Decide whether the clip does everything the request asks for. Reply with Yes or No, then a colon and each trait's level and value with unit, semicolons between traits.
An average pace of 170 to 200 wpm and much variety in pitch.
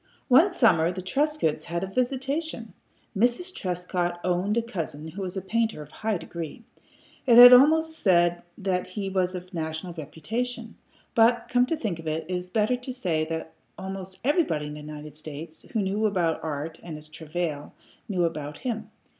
Yes: average, 180 wpm; wide, 6.4 semitones